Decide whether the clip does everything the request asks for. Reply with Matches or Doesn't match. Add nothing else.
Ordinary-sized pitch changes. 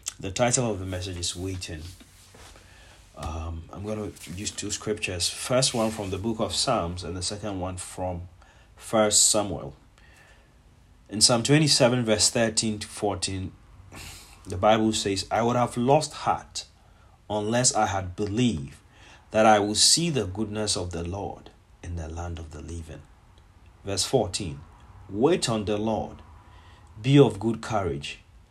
Matches